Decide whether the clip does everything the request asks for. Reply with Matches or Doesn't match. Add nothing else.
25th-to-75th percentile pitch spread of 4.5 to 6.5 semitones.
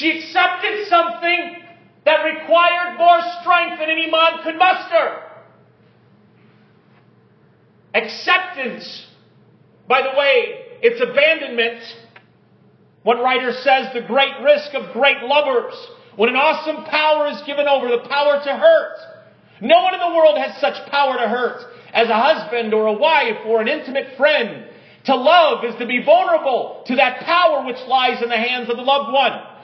Matches